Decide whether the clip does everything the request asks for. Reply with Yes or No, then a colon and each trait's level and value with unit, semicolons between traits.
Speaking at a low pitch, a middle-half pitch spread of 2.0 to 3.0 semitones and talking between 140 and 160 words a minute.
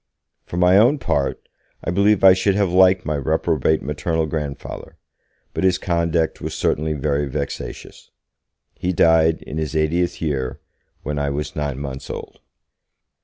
No: very low, 80 Hz; average, 3.5 semitones; average, 150 wpm